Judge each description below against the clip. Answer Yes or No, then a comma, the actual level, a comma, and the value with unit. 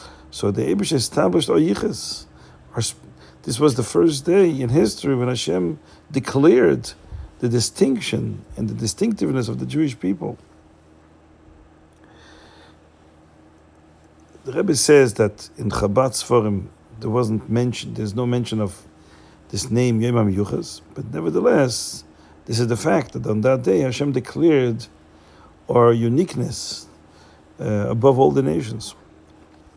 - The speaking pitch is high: No, low, 105 Hz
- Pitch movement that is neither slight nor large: No, wide, 7.7 semitones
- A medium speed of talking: Yes, average, 125 wpm